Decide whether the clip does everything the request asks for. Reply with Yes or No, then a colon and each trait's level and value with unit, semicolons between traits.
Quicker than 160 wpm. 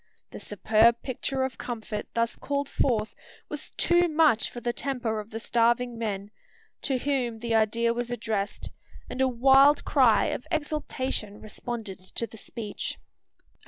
No: average, 150 wpm